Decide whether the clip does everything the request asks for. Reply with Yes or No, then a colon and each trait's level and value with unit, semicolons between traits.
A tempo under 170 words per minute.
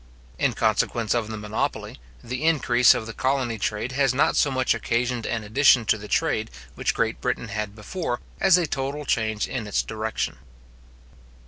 No: average, 175 wpm